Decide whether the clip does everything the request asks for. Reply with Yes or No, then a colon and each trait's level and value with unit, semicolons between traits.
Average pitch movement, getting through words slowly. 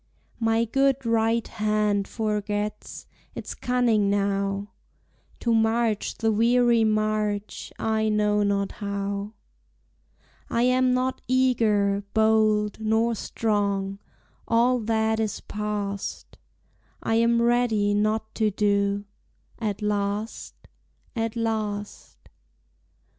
No: narrow, 1.9 semitones; slow, 100 wpm